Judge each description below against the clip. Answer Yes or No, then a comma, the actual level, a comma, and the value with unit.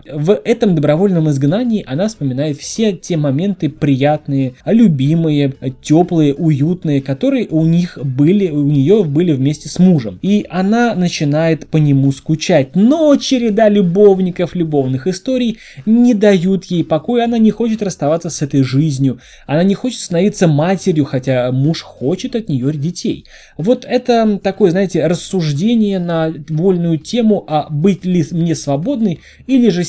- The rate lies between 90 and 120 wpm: No, average, 145 wpm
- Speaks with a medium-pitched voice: Yes, medium, 170 Hz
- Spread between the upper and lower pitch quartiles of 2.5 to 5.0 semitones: No, wide, 5.5 semitones